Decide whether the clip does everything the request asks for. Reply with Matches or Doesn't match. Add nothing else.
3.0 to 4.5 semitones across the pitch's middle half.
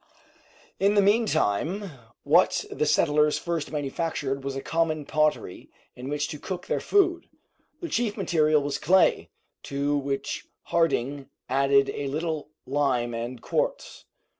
Matches